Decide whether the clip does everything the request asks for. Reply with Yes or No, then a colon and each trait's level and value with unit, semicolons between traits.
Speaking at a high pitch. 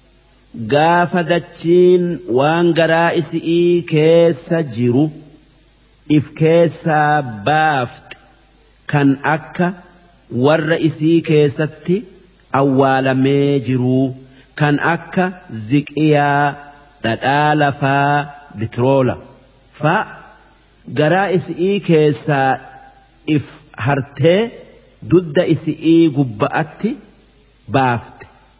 No: medium, 155 Hz